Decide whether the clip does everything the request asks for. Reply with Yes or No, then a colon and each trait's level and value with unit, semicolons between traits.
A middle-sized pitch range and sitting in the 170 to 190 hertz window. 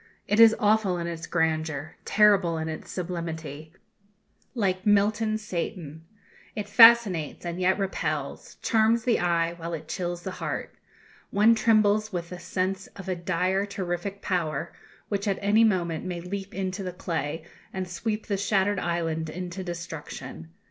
Yes: average, 3.3 semitones; medium, 185 Hz